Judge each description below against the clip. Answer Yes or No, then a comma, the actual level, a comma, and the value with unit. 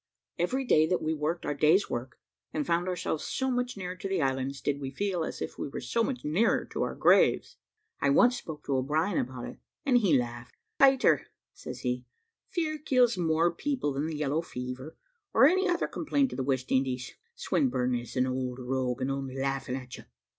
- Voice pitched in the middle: Yes, medium, 155 Hz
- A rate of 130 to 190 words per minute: No, fast, 205 wpm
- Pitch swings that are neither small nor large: No, wide, 7.6 semitones